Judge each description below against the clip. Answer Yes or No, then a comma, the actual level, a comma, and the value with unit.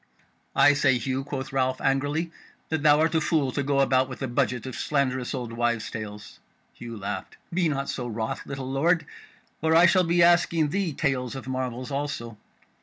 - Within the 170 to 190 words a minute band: Yes, average, 185 wpm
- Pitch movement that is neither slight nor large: Yes, average, 3.5 semitones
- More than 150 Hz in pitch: No, low, 135 Hz